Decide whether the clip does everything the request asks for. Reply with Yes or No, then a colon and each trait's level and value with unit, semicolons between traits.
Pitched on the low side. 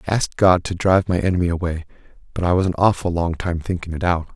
Yes: very low, 90 Hz